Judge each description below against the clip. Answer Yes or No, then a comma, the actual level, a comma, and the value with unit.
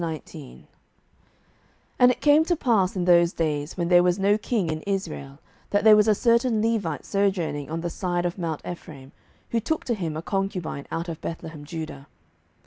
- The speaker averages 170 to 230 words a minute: Yes, average, 180 wpm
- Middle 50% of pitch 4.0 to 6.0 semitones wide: Yes, average, 4.5 semitones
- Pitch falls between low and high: Yes, medium, 175 Hz